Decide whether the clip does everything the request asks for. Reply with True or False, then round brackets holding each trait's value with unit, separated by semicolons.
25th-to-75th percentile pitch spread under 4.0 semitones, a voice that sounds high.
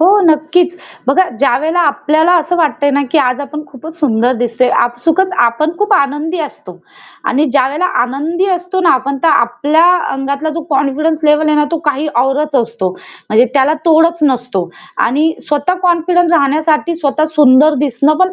True (3.4 semitones; 300 Hz)